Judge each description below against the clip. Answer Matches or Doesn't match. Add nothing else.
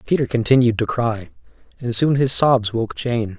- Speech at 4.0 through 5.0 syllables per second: Matches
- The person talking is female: Doesn't match